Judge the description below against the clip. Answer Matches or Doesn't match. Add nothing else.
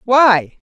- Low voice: Doesn't match